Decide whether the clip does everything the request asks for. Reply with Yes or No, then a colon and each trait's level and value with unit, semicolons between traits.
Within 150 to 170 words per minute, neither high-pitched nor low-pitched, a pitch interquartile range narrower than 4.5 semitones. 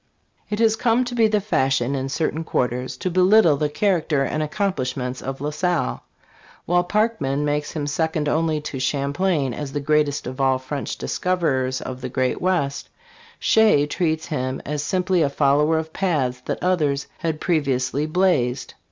No: average, 165 wpm; medium, 150 Hz; average, 4.8 semitones